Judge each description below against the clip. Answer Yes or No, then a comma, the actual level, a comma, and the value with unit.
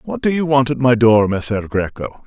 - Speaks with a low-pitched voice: Yes, low, 125 Hz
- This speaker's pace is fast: Yes, fast, 240 wpm